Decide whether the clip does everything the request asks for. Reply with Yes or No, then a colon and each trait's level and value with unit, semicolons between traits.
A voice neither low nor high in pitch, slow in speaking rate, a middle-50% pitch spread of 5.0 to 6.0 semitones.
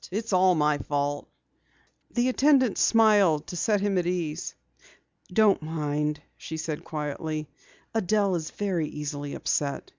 Yes: medium, 165 Hz; slow, 130 wpm; average, 5.3 semitones